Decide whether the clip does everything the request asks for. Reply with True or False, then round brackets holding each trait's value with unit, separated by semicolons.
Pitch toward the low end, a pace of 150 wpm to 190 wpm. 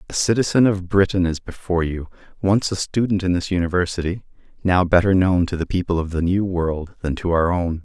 False (90 Hz; 205 wpm)